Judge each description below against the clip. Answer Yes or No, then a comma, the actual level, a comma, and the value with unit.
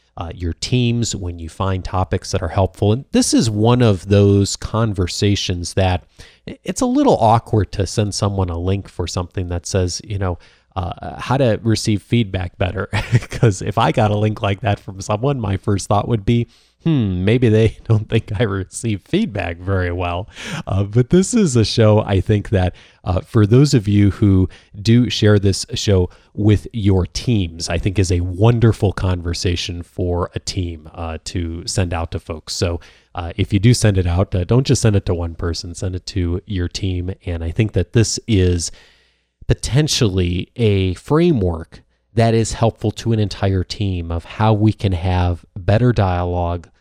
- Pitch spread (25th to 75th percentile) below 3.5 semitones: No, average, 3.8 semitones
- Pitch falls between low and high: No, low, 100 Hz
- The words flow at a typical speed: Yes, average, 185 wpm